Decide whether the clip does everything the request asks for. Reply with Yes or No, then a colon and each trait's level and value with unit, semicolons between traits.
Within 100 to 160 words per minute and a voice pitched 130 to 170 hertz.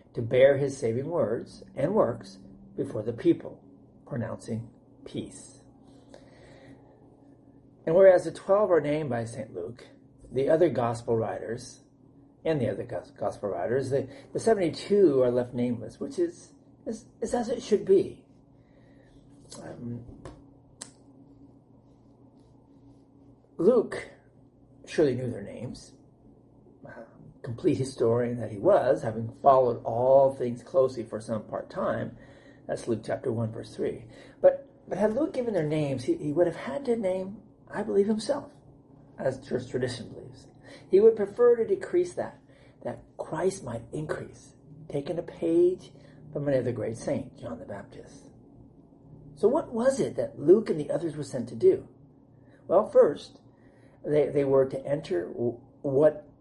Yes: average, 140 wpm; medium, 140 Hz